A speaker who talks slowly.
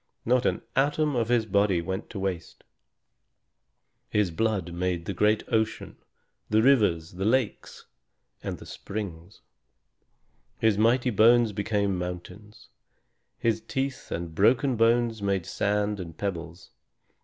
Yes: slow, 120 wpm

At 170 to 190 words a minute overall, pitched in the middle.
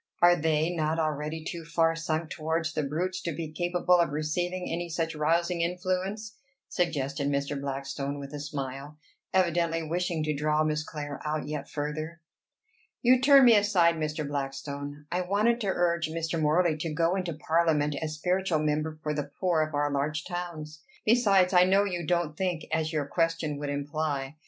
Yes: average, 175 wpm; medium, 160 Hz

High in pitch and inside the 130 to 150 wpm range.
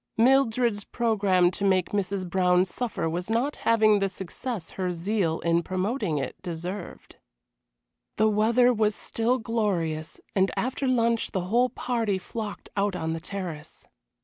Yes: high, 200 Hz; average, 145 wpm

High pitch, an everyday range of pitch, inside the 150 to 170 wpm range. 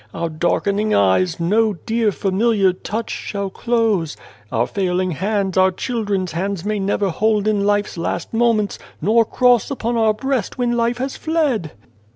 Yes: high, 205 Hz; average, 3.6 semitones; average, 155 wpm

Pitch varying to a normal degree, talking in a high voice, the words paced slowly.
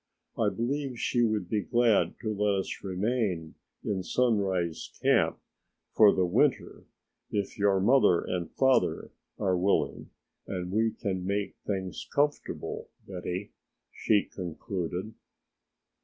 No: average, 3.6 semitones; low, 100 Hz; slow, 120 wpm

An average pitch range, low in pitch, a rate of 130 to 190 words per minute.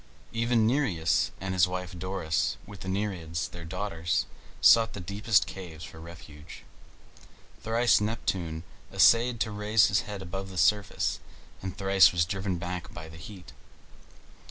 Yes: average, 3.7 semitones; very low, 95 Hz; average, 145 wpm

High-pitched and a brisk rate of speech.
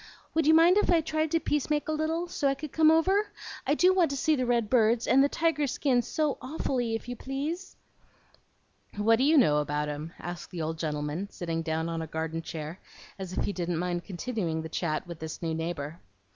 Yes: high, 225 Hz; fast, 220 wpm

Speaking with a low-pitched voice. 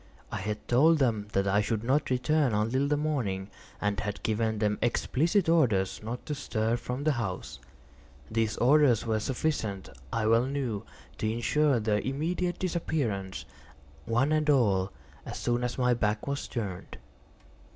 Yes: low, 120 Hz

